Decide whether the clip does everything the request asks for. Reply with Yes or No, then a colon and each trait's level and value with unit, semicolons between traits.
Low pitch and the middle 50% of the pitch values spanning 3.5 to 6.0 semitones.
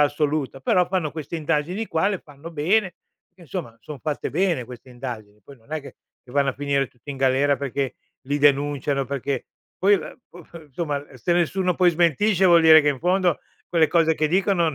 No: medium, 150 Hz; average, 3.9 semitones